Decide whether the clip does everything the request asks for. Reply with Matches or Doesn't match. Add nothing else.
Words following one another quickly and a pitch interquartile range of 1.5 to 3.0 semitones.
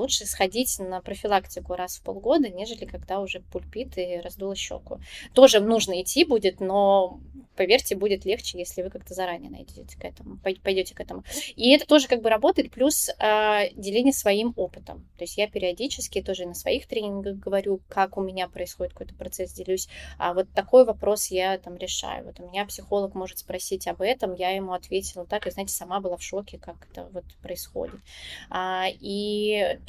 Matches